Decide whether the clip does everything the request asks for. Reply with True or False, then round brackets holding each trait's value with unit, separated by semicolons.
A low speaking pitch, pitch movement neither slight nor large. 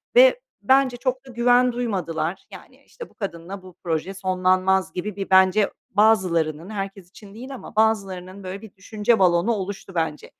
False (195 Hz; 3.4 semitones)